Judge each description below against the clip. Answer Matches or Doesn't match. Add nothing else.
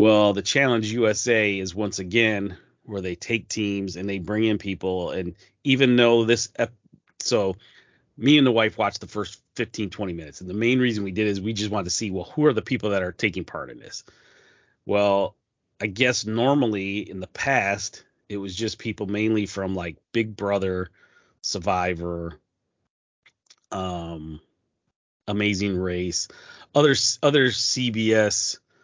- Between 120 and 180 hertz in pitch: Doesn't match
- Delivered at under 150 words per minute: Doesn't match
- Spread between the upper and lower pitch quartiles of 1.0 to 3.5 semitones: Matches